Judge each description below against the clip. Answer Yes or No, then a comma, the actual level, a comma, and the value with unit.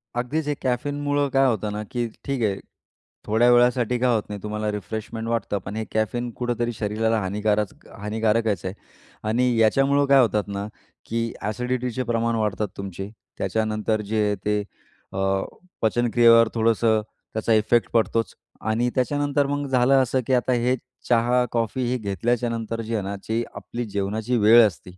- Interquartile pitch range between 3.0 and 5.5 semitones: No, narrow, 2.6 semitones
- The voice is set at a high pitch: No, low, 115 Hz